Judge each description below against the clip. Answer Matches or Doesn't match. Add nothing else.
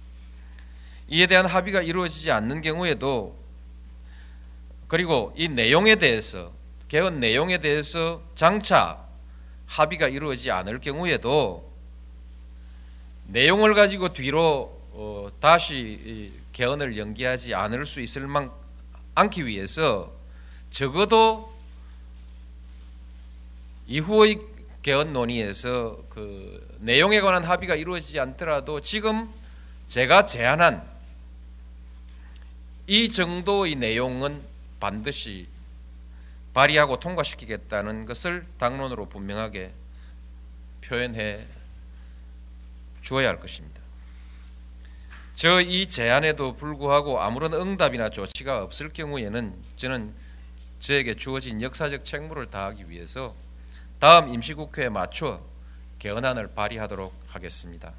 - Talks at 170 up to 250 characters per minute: Matches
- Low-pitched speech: Matches